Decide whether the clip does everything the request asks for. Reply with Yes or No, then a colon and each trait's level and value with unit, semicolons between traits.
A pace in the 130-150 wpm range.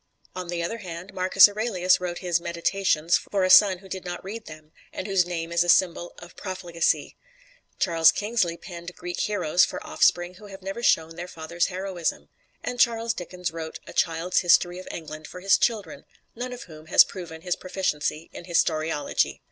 No: average, 185 wpm